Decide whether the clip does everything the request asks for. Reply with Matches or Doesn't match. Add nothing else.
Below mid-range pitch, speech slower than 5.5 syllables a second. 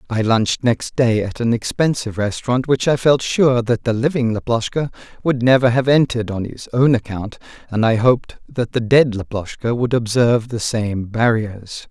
Matches